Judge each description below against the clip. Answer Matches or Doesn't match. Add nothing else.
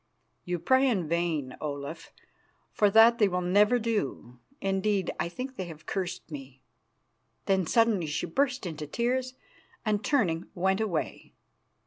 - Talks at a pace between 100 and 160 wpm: Matches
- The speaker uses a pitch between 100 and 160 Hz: Doesn't match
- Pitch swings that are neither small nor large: Doesn't match